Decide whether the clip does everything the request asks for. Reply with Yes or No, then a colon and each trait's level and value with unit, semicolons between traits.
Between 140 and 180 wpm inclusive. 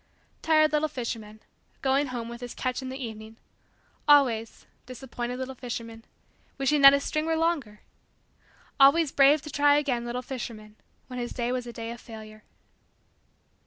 Yes: average, 160 wpm